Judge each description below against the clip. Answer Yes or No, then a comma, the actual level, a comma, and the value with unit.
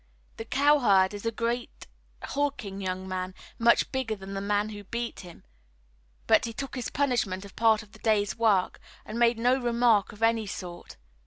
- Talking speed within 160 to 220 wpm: Yes, average, 180 wpm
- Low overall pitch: No, high, 220 Hz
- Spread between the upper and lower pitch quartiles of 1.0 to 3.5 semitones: Yes, average, 3.2 semitones